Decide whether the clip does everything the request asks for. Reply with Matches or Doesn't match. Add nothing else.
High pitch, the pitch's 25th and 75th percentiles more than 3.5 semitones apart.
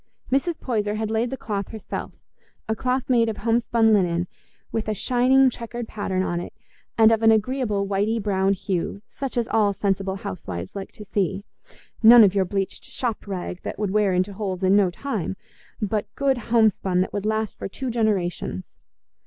Doesn't match